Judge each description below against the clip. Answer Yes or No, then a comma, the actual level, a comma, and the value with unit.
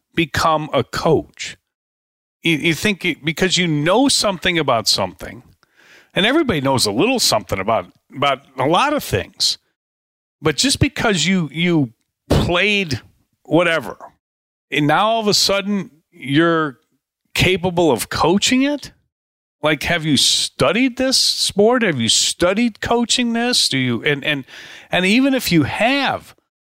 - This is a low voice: No, medium, 170 Hz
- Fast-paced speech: No, average, 140 wpm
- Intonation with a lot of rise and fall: Yes, wide, 7.1 semitones